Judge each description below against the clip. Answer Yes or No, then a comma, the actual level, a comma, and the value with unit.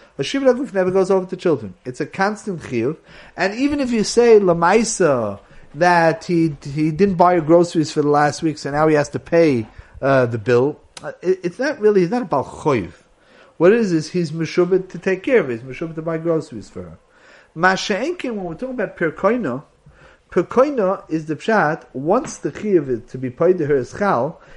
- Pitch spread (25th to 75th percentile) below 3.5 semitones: No, average, 4.3 semitones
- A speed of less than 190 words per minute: No, fast, 205 wpm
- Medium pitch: Yes, medium, 170 Hz